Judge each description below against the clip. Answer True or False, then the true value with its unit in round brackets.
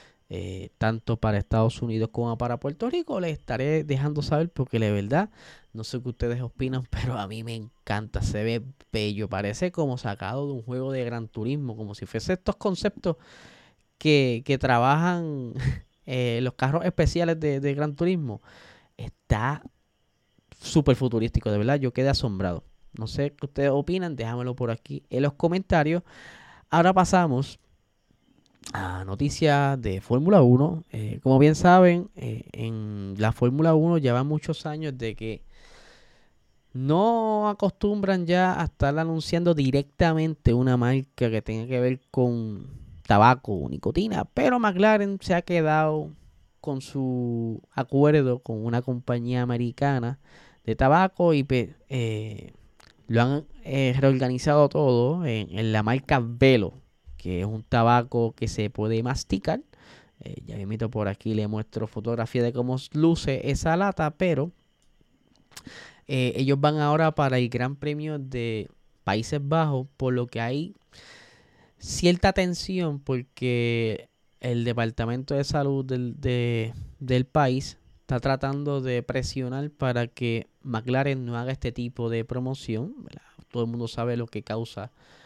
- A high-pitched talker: False (130 Hz)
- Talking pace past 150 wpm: False (145 wpm)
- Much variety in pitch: False (4.6 semitones)